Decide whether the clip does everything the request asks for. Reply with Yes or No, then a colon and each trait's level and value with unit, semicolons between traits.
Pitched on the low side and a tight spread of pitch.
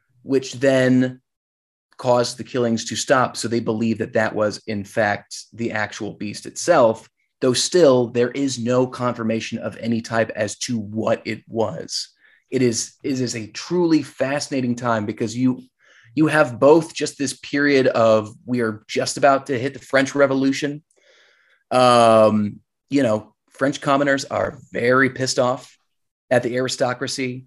No: low, 125 Hz; average, 3.1 semitones